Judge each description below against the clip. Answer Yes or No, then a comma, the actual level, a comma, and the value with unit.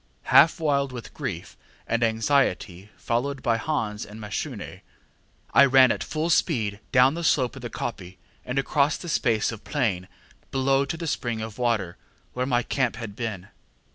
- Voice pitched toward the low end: Yes, low, 120 Hz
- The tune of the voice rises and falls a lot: No, average, 3.9 semitones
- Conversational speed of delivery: Yes, average, 170 wpm